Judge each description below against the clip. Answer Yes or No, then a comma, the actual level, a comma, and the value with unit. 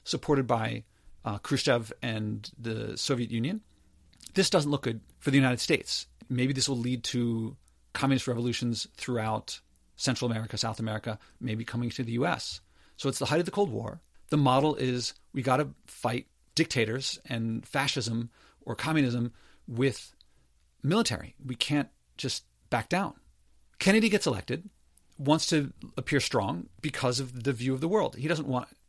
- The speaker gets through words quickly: No, average, 160 wpm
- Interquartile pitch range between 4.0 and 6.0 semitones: No, average, 3.5 semitones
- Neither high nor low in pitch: No, low, 125 Hz